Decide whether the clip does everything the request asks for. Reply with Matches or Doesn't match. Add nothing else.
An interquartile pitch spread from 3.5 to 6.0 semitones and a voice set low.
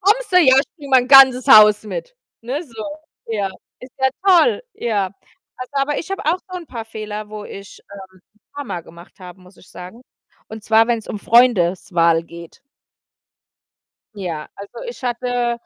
Doesn't match